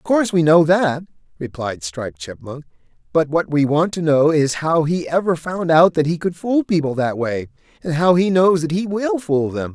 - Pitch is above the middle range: No, medium, 160 Hz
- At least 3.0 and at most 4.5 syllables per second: No, 4.9 syllables/s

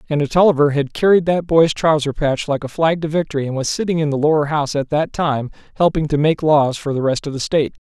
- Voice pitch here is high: No, medium, 150 Hz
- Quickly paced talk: Yes, fast, 260 wpm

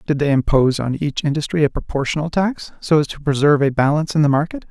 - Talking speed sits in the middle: No, fast, 230 wpm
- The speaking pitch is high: No, medium, 150 Hz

